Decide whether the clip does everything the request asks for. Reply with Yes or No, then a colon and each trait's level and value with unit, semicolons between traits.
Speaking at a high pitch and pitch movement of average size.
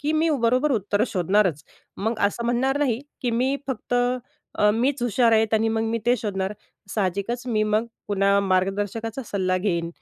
Yes: high, 220 Hz; average, 3.4 semitones